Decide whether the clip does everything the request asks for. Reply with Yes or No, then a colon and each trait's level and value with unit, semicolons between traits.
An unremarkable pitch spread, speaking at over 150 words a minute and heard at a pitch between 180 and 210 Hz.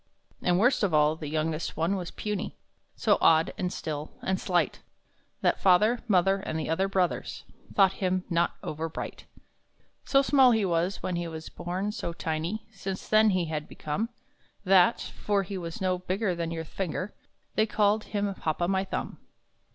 Yes: average, 3.4 semitones; average, 175 wpm; medium, 185 Hz